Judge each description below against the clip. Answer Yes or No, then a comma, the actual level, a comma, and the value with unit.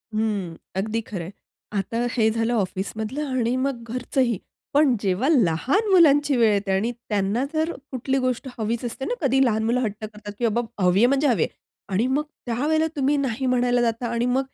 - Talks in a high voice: Yes, high, 235 Hz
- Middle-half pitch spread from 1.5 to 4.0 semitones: Yes, average, 3.7 semitones